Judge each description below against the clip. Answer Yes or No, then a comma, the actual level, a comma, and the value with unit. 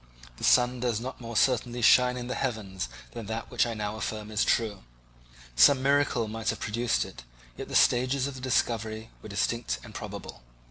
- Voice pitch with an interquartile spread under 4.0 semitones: Yes, narrow, 2.5 semitones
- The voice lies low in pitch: Yes, low, 115 Hz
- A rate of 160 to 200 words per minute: Yes, average, 190 wpm